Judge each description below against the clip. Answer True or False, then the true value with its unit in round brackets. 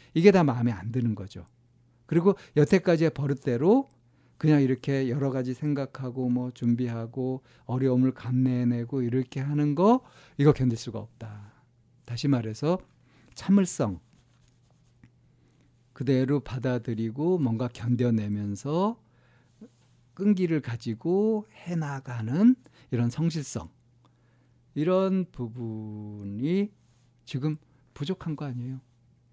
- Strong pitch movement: False (3.7 semitones)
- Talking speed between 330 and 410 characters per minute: False (240 characters per minute)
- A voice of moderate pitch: False (130 Hz)